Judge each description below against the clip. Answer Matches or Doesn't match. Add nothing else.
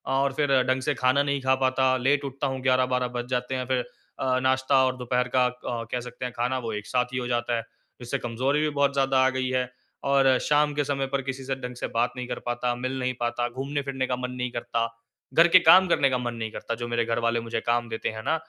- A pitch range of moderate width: Doesn't match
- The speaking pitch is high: Doesn't match